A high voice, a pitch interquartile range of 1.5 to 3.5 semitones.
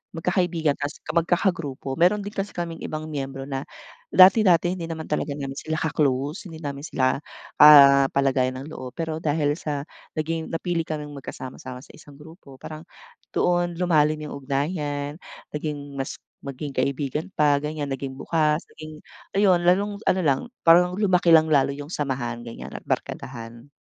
No: medium, 150 Hz; average, 3.2 semitones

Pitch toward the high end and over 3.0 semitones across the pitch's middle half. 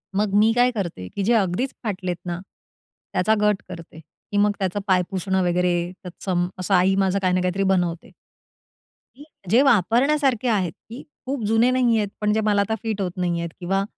Yes: high, 195 Hz; average, 3.6 semitones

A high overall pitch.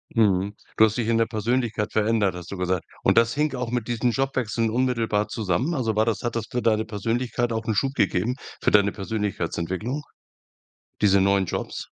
No: low, 110 Hz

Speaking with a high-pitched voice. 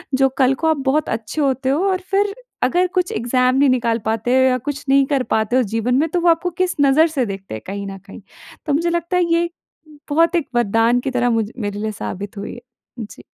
Yes: very high, 260 Hz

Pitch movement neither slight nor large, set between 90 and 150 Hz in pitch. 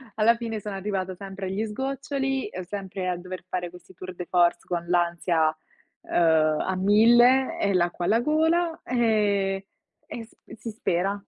No: average, 4.4 semitones; high, 200 Hz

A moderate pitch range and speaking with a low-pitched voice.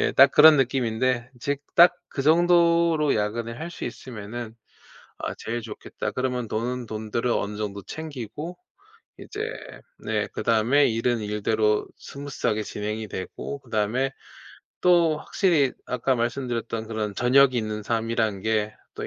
Yes: average, 4.3 semitones; low, 120 Hz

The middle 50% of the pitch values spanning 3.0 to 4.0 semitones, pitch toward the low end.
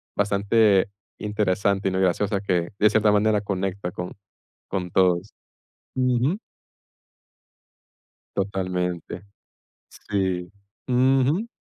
No: narrow, 2.5 semitones; low, 100 Hz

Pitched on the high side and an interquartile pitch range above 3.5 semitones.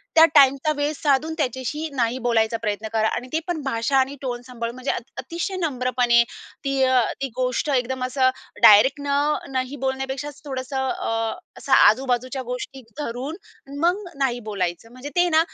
No: very high, 260 Hz; average, 2.8 semitones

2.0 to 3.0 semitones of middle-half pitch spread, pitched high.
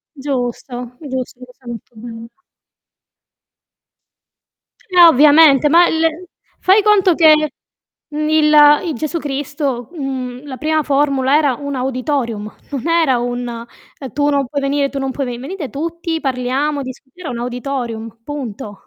No: average, 3.6 semitones; very high, 275 Hz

